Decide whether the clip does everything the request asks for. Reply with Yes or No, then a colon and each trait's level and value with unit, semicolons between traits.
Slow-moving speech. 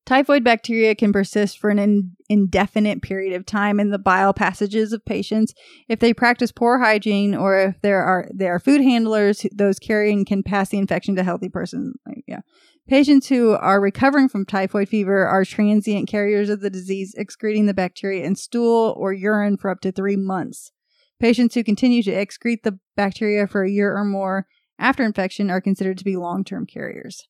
No: average, 185 wpm